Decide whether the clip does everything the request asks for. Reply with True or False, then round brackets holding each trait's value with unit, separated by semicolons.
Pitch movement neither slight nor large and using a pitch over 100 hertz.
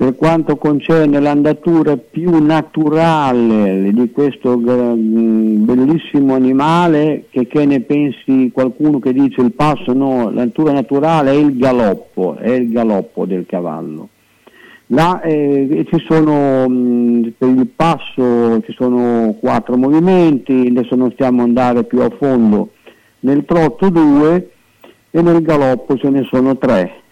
True (3.6 semitones; 135 Hz)